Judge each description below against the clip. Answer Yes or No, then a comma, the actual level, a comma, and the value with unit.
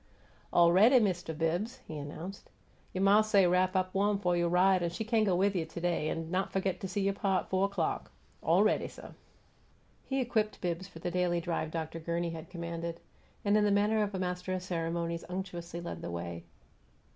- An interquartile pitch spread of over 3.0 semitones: No, average, 2.7 semitones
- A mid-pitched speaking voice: Yes, medium, 180 Hz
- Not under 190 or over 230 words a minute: Yes, fast, 205 wpm